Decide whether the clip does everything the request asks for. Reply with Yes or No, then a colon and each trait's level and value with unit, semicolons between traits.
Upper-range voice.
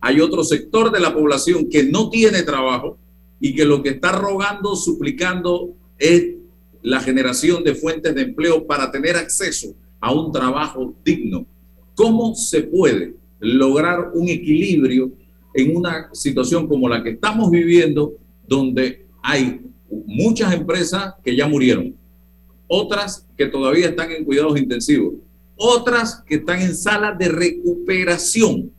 No: medium, 155 Hz